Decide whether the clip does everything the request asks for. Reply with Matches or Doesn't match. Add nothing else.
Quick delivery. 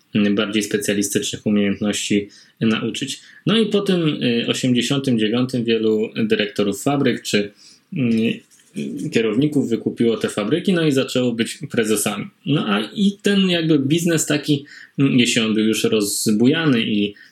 Doesn't match